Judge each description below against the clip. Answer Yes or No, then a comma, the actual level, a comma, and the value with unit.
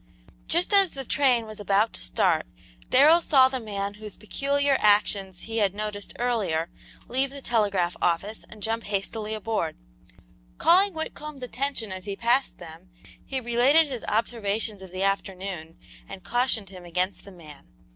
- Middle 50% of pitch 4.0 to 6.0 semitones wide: Yes, average, 4.8 semitones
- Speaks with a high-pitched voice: Yes, high, 215 Hz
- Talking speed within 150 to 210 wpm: Yes, average, 155 wpm